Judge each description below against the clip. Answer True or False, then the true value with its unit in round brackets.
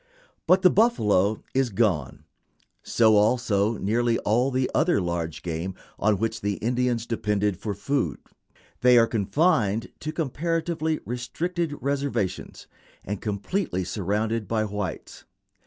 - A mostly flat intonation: False (5.1 semitones)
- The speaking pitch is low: True (115 Hz)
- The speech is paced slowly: True (125 wpm)